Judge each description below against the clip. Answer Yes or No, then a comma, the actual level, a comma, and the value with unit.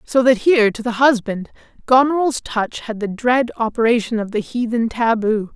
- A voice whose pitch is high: Yes, high, 235 Hz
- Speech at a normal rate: Yes, average, 175 wpm